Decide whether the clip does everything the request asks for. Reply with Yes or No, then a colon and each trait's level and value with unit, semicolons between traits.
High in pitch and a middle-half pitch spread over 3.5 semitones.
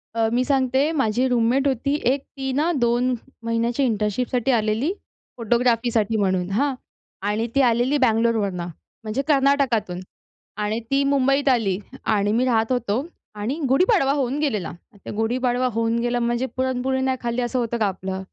No: high, 240 Hz; average, 3.2 semitones